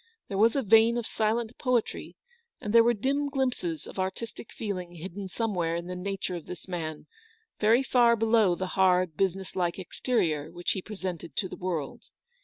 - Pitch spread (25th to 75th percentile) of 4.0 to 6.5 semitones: Yes, average, 4.5 semitones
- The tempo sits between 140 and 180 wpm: No, average, 200 wpm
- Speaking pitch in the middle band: No, high, 195 Hz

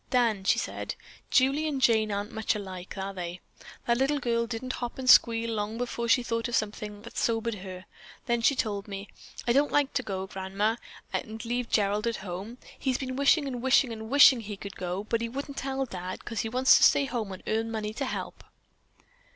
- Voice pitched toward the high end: Yes, high, 230 Hz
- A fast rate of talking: Yes, fast, 210 wpm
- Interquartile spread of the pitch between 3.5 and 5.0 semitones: Yes, average, 3.8 semitones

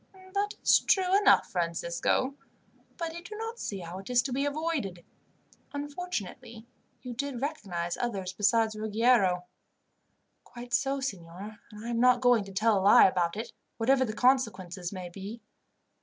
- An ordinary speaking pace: Yes, average, 155 wpm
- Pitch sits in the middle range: No, high, 230 Hz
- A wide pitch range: Yes, wide, 6.1 semitones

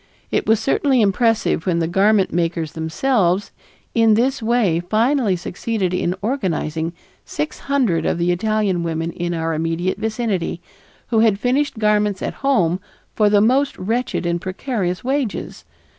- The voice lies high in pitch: Yes, high, 200 Hz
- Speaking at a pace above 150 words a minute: No, average, 145 wpm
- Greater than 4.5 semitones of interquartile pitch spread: Yes, average, 4.9 semitones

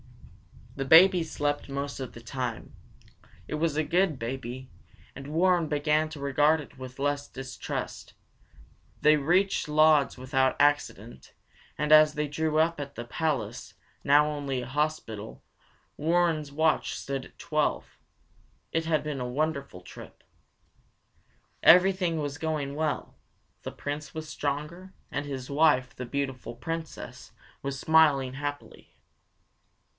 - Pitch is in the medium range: Yes, medium, 145 Hz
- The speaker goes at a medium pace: No, slow, 130 wpm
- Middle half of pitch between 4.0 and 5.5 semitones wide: No, average, 2.8 semitones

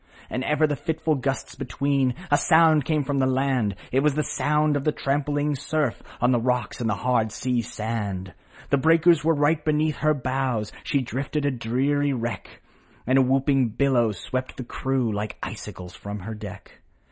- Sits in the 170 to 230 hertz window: No, low, 135 Hz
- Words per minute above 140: Yes, average, 180 wpm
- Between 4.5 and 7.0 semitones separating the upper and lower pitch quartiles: No, average, 3.5 semitones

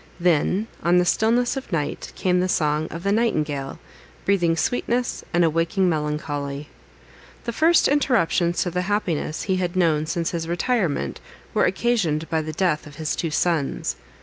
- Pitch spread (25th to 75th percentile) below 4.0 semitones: No, average, 4.3 semitones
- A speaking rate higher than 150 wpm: Yes, average, 160 wpm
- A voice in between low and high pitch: Yes, medium, 170 Hz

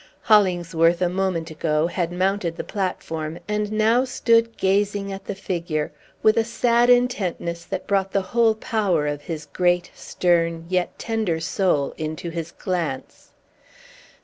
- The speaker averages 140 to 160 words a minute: Yes, average, 145 wpm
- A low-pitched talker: No, medium, 185 Hz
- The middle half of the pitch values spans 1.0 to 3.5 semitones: No, average, 3.9 semitones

